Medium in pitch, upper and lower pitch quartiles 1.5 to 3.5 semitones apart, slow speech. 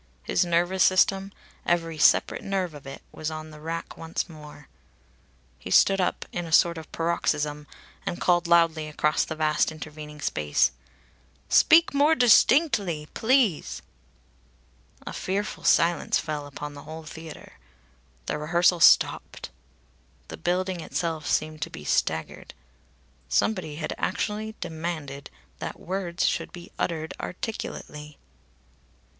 Yes: medium, 165 Hz; average, 3.1 semitones; slow, 125 wpm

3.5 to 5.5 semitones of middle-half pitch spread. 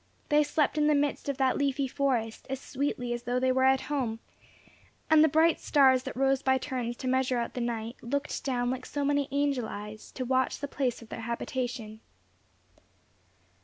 No: narrow, 2.6 semitones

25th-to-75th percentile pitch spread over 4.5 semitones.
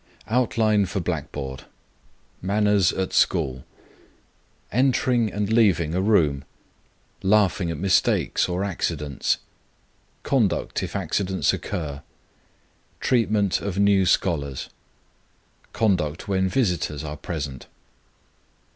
Yes: average, 4.9 semitones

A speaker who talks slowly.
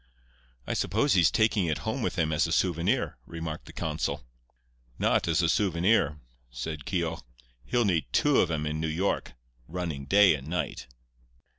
No: average, 165 wpm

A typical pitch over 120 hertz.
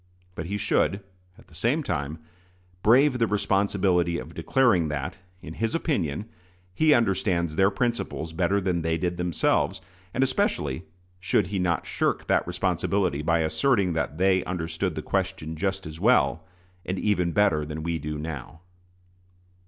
No: very low, 90 Hz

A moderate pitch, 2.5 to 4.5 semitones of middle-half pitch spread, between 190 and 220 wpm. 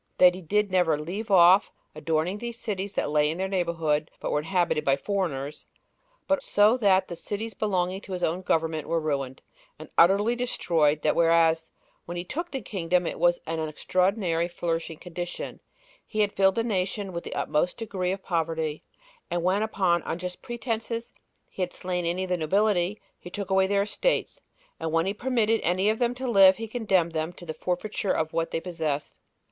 Yes: medium, 180 Hz; average, 3.8 semitones; average, 195 wpm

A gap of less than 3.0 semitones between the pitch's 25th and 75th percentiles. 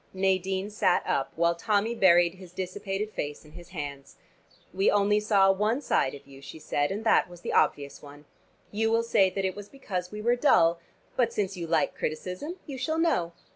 No: average, 3.9 semitones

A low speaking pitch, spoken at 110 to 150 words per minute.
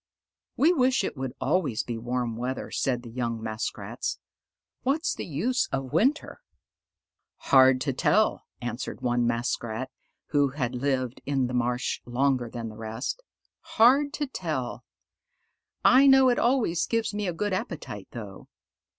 Yes: low, 130 Hz; average, 145 wpm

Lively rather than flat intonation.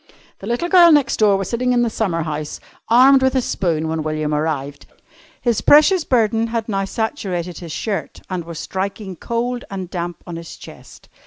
Yes: wide, 6.2 semitones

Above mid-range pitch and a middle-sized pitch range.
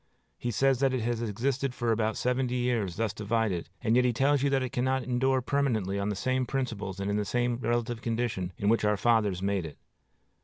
No: low, 120 Hz; average, 3.5 semitones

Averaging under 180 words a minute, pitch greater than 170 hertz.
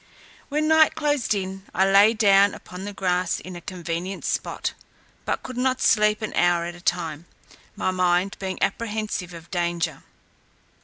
Yes: average, 160 wpm; high, 190 Hz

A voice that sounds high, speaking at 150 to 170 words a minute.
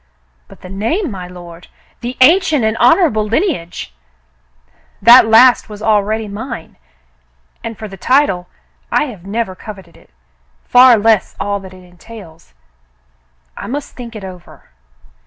Yes: high, 215 Hz; average, 155 wpm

